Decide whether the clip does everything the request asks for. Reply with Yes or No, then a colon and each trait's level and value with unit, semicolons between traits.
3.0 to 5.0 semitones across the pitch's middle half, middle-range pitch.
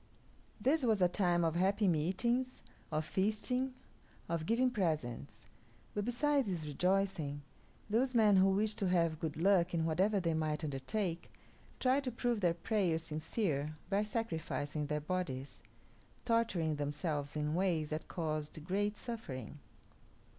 No: wide, 5.6 semitones; medium, 180 Hz